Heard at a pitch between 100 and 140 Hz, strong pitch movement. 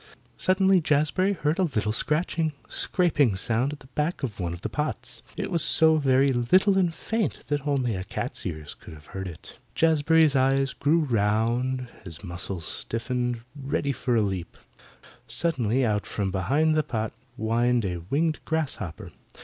Yes: low, 135 Hz; wide, 6.4 semitones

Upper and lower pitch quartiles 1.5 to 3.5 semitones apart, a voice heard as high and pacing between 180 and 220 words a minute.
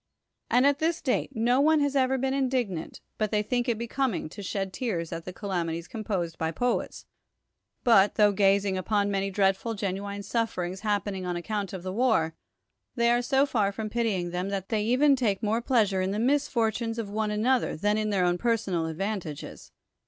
No: average, 3.9 semitones; high, 210 Hz; average, 190 wpm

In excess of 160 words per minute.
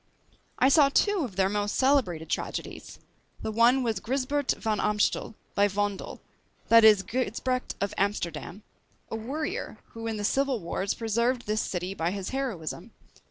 No: average, 155 wpm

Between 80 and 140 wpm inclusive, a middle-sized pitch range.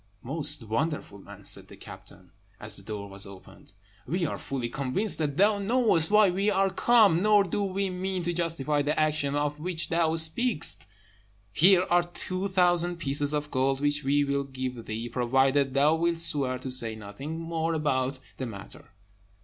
No: average, 175 wpm; average, 5.0 semitones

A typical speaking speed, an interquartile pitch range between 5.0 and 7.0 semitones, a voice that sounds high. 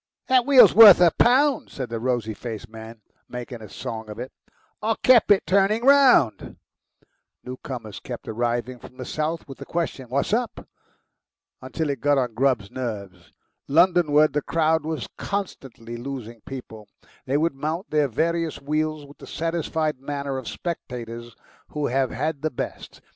No: average, 160 wpm; wide, 5.5 semitones; medium, 140 Hz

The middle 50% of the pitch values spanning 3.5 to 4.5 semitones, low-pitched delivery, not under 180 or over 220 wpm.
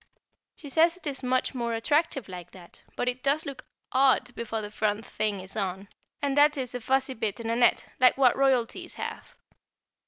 No: average, 4.1 semitones; very high, 250 Hz; average, 195 wpm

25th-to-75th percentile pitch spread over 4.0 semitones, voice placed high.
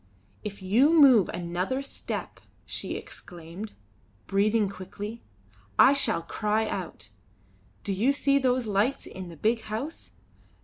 Yes: average, 5.1 semitones; high, 215 Hz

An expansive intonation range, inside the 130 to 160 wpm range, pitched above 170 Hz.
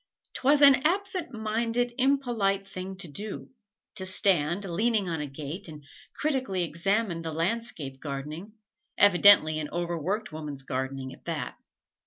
Yes: wide, 6.6 semitones; average, 140 wpm; high, 190 Hz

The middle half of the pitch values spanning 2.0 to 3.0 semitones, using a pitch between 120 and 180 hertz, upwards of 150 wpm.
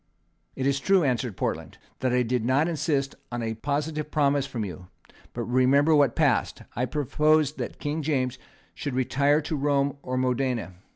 Yes: average, 2.7 semitones; low, 135 Hz; average, 170 wpm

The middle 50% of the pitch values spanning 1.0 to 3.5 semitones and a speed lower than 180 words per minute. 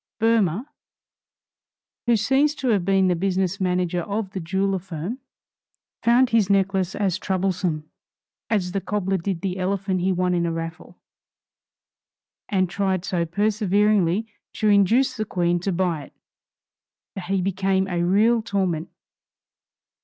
Yes: narrow, 2.4 semitones; average, 140 wpm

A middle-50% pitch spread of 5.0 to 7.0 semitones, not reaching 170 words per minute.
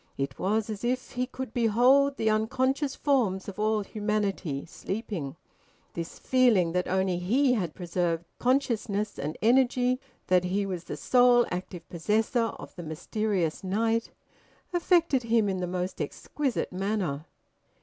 Yes: average, 5.3 semitones; average, 140 wpm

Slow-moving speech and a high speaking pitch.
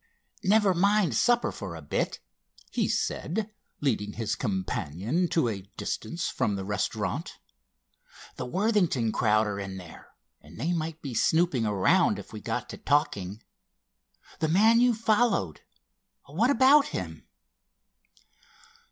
No: slow, 125 wpm; low, 135 Hz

